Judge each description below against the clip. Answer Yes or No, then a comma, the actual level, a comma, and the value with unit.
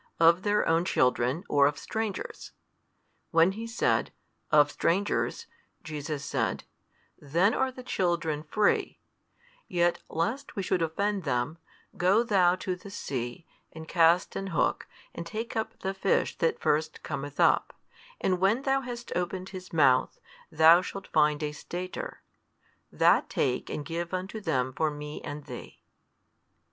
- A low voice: No, medium, 170 Hz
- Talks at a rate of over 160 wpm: No, average, 145 wpm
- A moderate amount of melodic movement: Yes, average, 4.4 semitones